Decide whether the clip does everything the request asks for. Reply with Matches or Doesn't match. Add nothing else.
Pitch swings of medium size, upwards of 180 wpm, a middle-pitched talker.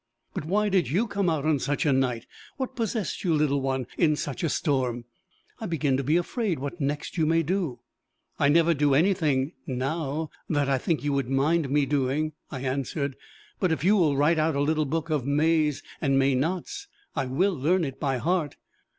Matches